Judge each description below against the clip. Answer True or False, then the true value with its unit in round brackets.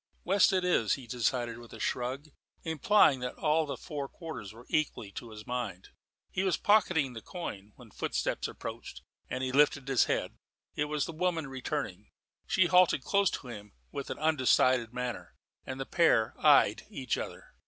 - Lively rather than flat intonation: False (5.0 semitones)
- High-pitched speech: False (135 Hz)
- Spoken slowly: False (175 wpm)